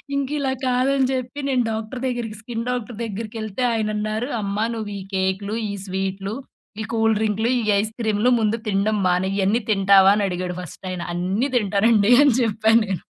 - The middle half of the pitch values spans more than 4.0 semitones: No, average, 3.1 semitones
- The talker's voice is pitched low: No, high, 215 Hz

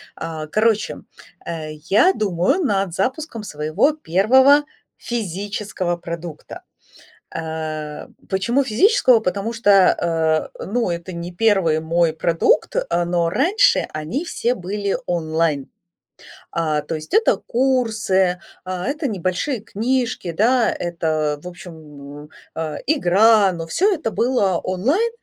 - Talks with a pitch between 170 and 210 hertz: Yes, medium, 185 Hz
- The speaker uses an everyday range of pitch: No, wide, 6.0 semitones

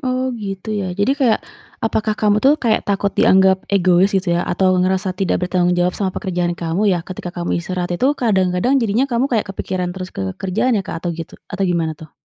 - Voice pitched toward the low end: No, high, 190 Hz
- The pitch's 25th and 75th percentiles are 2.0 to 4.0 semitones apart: Yes, average, 3.2 semitones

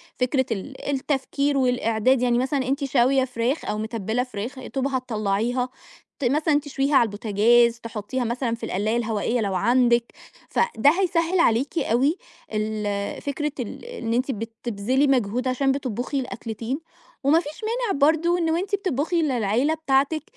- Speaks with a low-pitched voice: No, very high, 255 Hz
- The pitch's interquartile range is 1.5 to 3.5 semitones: No, average, 3.9 semitones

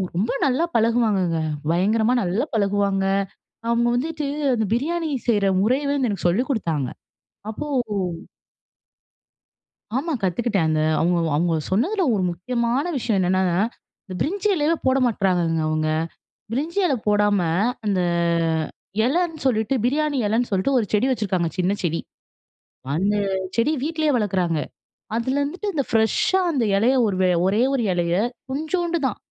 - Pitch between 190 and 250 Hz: Yes, high, 225 Hz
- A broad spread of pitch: Yes, wide, 6.5 semitones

